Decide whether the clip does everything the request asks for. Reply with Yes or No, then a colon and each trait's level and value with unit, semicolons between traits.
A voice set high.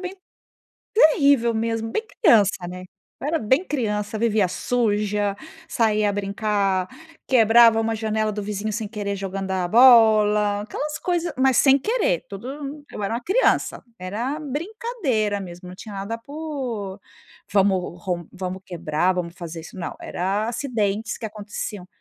Yes: high, 215 Hz